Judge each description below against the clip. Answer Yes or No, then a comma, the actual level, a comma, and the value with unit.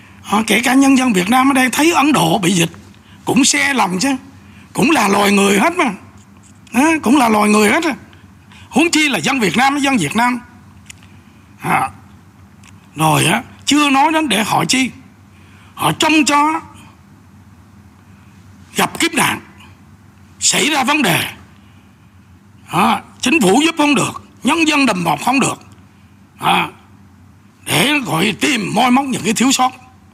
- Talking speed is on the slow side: Yes, slow, 150 wpm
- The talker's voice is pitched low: No, medium, 180 Hz